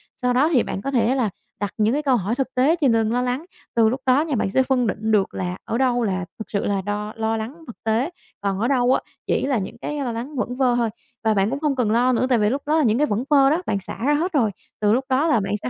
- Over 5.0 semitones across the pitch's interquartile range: No, average, 3.8 semitones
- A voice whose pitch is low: No, high, 245 Hz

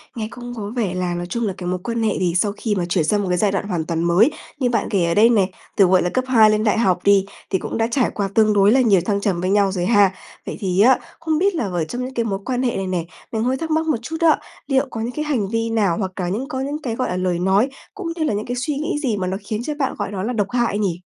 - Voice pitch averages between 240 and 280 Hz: No, high, 210 Hz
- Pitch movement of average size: Yes, average, 4.6 semitones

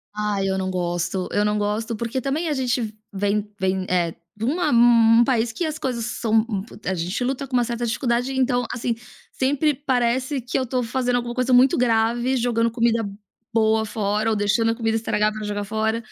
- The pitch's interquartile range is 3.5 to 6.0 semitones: No, average, 2.9 semitones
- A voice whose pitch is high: Yes, high, 230 Hz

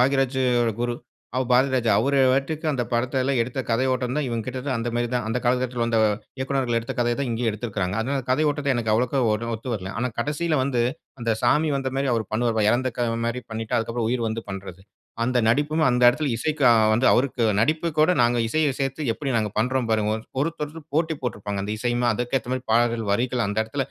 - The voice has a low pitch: Yes, low, 125 Hz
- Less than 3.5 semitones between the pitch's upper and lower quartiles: Yes, average, 2.8 semitones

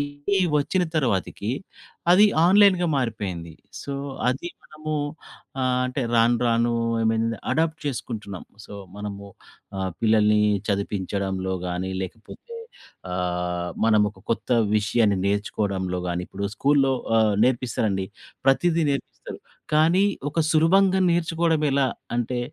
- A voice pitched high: No, low, 115 Hz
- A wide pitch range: Yes, wide, 7.0 semitones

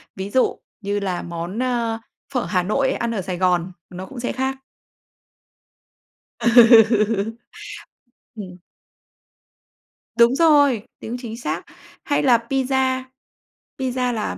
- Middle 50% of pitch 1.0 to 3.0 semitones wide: No, average, 4.4 semitones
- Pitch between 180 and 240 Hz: Yes, high, 230 Hz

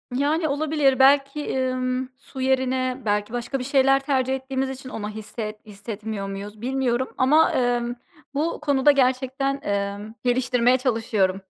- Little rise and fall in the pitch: No, average, 3.3 semitones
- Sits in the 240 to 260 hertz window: Yes, very high, 255 Hz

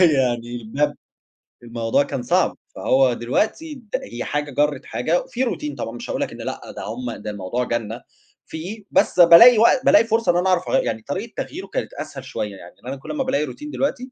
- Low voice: No, medium, 145 Hz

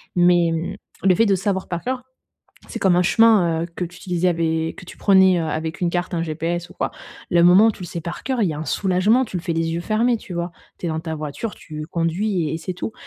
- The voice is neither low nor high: Yes, medium, 175 Hz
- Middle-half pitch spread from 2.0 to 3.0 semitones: Yes, average, 2.7 semitones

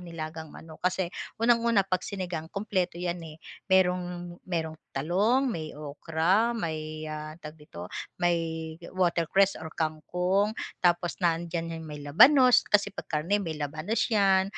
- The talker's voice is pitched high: No, medium, 175 Hz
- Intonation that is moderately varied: Yes, average, 3.5 semitones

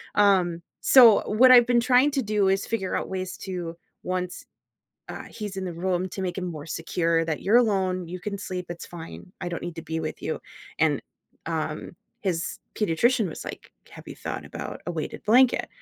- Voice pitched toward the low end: No, medium, 185 Hz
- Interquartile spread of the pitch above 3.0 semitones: Yes, average, 3.4 semitones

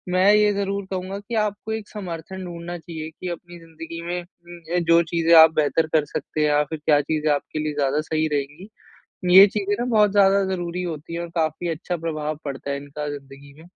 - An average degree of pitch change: Yes, average, 3.5 semitones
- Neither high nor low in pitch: Yes, medium, 170 Hz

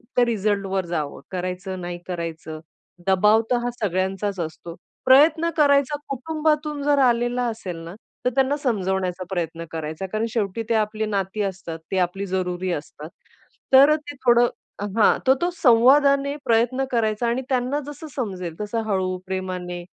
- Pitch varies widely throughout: Yes, wide, 5.9 semitones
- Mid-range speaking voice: No, high, 210 Hz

